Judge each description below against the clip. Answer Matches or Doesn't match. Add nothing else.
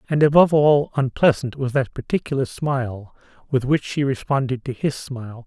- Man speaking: Matches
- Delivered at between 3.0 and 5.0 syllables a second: Doesn't match